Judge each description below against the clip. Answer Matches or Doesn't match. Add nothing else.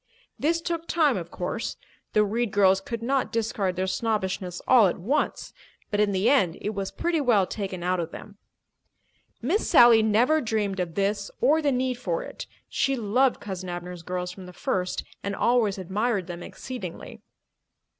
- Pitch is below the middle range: Doesn't match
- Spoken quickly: Doesn't match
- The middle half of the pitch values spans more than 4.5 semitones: Matches